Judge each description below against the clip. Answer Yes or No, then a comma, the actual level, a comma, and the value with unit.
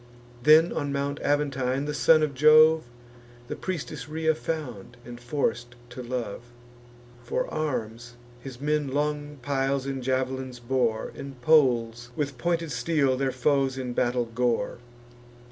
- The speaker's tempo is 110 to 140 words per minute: Yes, slow, 135 wpm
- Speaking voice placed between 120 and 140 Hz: Yes, low, 135 Hz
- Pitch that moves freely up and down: No, average, 3.3 semitones